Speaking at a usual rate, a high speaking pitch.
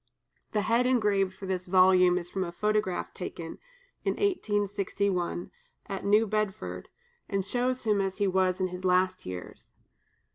Yes: average, 150 wpm; high, 195 Hz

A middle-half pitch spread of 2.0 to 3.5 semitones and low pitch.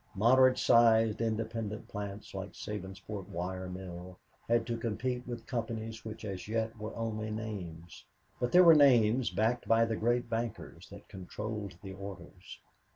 Yes: average, 2.9 semitones; low, 110 Hz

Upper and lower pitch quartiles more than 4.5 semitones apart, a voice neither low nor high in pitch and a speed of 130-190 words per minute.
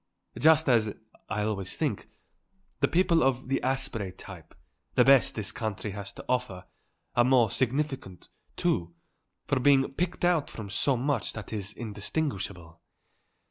No: average, 5.1 semitones; low, 120 Hz; average, 140 wpm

